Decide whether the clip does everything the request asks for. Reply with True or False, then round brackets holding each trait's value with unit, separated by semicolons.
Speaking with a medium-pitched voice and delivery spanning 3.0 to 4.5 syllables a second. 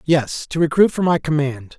False (150 Hz; 4.9 syllables/s)